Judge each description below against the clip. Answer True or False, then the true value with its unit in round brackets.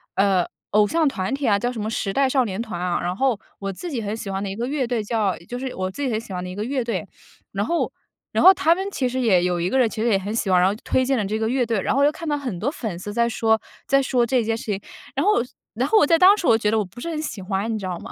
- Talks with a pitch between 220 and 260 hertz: True (225 Hz)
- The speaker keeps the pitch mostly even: False (5.1 semitones)